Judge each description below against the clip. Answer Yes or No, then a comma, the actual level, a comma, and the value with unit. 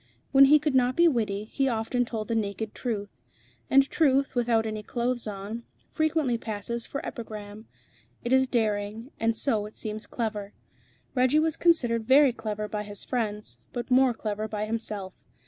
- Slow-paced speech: No, average, 165 wpm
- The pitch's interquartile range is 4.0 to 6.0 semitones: No, average, 3.4 semitones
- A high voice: Yes, high, 230 Hz